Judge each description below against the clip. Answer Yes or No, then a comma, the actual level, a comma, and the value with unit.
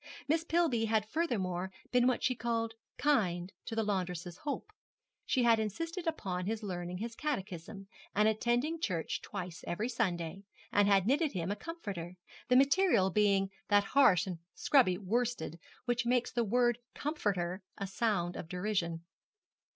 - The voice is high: Yes, high, 210 Hz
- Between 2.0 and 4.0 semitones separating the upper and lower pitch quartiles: No, average, 5.2 semitones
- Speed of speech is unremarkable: Yes, average, 155 wpm